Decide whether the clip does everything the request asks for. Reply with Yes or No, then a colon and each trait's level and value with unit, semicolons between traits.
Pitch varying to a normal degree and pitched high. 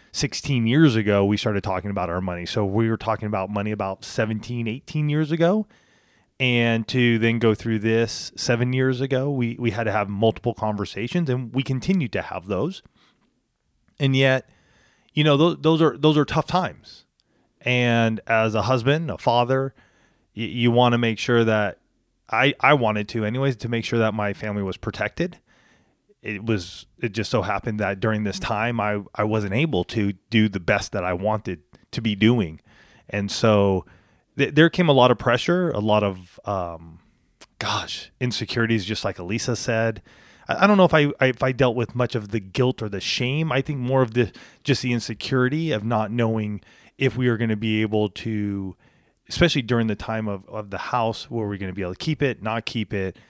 No: average, 3.6 semitones; low, 115 Hz